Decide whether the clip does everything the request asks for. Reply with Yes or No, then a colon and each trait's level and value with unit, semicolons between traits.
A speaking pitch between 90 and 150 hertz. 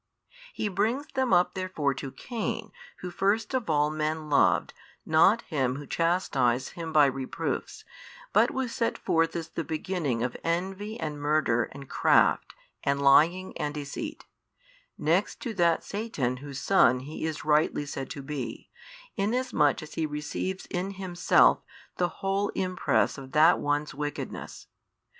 No: medium, 160 Hz